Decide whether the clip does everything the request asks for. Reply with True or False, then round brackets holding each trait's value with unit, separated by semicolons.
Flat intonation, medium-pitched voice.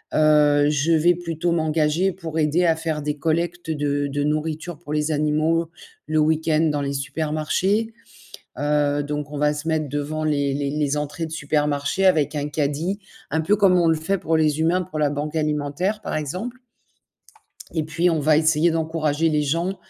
True (1.9 semitones; 155 Hz)